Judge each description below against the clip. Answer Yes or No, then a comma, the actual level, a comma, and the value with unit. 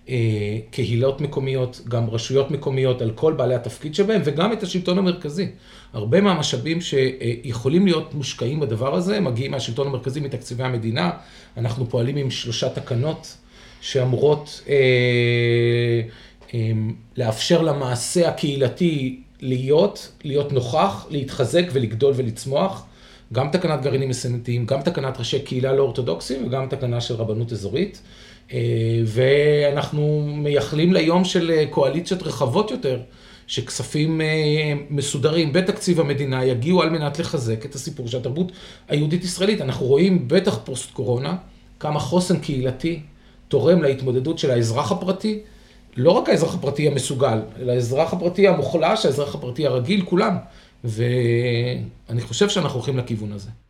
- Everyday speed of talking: Yes, average, 125 wpm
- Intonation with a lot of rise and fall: No, average, 4.7 semitones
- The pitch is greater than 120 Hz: Yes, low, 135 Hz